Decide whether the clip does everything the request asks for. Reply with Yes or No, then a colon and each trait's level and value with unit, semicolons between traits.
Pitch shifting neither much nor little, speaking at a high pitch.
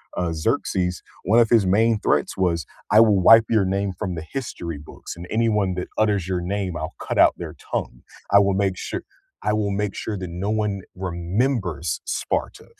No: average, 3.1 semitones; very low, 95 Hz